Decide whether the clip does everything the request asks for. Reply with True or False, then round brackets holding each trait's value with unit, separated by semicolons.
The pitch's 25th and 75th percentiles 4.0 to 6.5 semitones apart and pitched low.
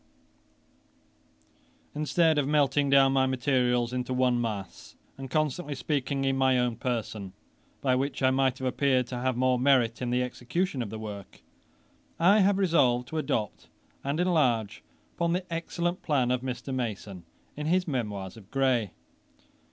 False (3.1 semitones; 130 Hz)